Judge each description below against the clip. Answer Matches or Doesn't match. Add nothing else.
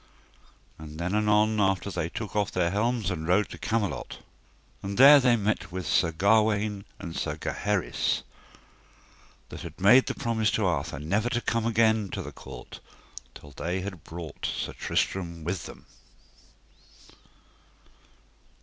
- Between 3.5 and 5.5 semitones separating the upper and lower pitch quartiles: Matches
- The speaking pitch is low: Matches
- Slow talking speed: Doesn't match